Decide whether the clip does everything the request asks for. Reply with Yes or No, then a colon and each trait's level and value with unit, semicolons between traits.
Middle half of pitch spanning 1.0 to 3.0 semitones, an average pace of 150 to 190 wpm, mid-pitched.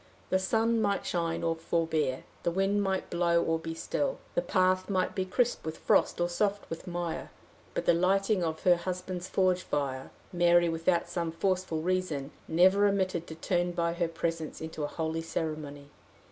Yes: narrow, 2.4 semitones; average, 175 wpm; medium, 175 Hz